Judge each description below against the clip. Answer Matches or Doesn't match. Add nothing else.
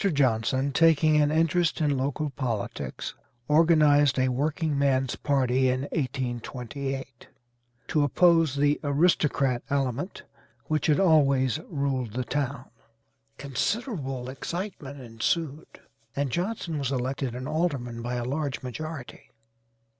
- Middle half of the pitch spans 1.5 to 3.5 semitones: Matches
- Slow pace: Matches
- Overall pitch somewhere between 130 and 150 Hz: Matches